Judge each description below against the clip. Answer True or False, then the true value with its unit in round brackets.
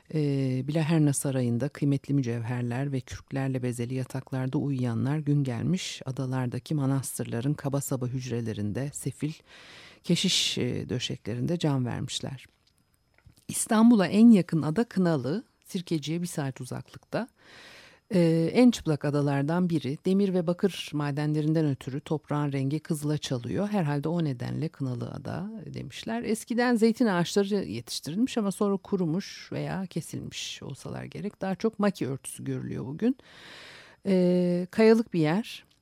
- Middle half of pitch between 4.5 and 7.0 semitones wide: True (5.5 semitones)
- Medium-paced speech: True (120 wpm)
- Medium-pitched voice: True (150 Hz)